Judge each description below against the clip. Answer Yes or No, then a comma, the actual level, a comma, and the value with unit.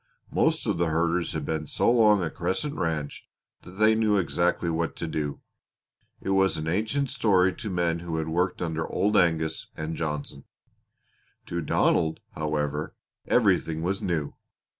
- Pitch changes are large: No, average, 3.3 semitones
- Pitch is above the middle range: No, very low, 85 Hz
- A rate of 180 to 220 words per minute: No, average, 160 wpm